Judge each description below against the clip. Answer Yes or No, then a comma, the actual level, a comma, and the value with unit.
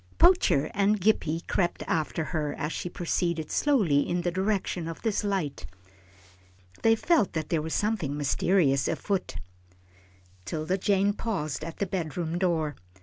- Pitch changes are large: No, average, 4.3 semitones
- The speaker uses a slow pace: No, average, 145 wpm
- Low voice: No, medium, 175 Hz